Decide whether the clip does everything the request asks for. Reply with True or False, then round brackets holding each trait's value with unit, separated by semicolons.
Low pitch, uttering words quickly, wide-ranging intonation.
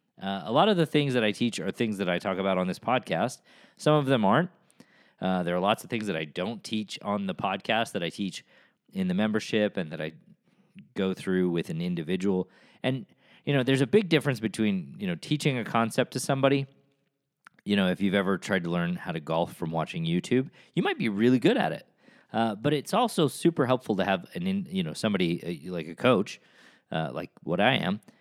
True (130 Hz; 230 wpm; 8.9 semitones)